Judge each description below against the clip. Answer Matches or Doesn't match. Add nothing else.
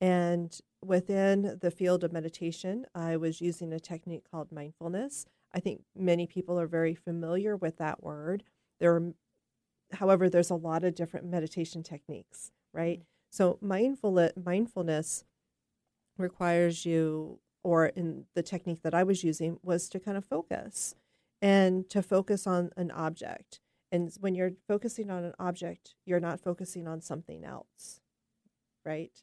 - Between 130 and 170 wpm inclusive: Matches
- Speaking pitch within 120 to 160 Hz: Doesn't match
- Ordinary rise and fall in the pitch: Doesn't match